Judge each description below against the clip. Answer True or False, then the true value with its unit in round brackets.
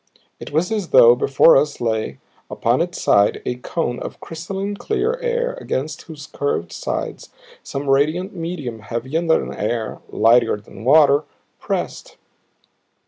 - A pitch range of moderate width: False (6.2 semitones)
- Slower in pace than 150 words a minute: True (140 wpm)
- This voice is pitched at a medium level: True (145 Hz)